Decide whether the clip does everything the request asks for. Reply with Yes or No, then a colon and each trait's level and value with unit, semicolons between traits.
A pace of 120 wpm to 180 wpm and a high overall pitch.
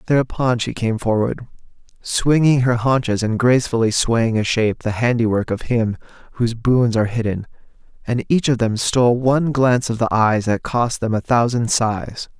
No: average, 175 wpm; low, 120 Hz